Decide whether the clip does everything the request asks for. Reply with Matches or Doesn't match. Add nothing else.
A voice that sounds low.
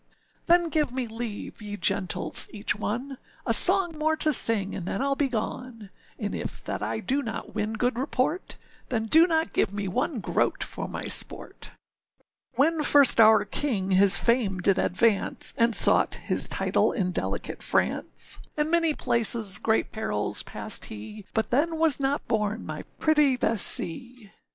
Doesn't match